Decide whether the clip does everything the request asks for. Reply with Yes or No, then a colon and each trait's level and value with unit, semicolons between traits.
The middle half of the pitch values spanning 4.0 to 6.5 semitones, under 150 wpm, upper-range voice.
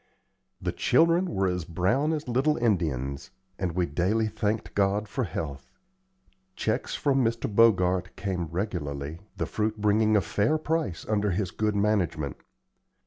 No: average, 4.3 semitones; average, 140 wpm; low, 100 Hz